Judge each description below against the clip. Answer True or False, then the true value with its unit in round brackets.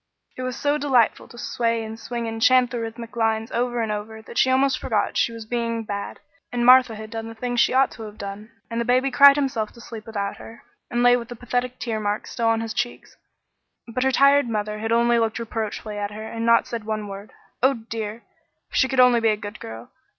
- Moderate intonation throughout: False (2.0 semitones)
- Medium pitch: False (230 Hz)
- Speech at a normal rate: False (240 wpm)